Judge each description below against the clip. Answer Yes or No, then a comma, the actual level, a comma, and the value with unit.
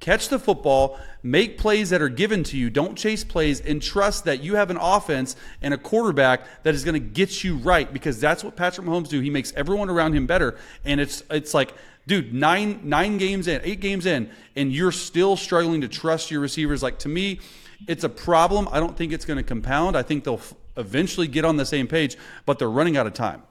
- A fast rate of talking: Yes, fast, 230 wpm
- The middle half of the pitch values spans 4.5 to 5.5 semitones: Yes, average, 5.0 semitones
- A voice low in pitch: No, medium, 165 Hz